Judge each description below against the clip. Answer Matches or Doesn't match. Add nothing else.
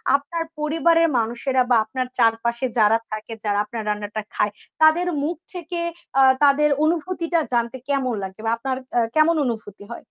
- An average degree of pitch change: Doesn't match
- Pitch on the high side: Matches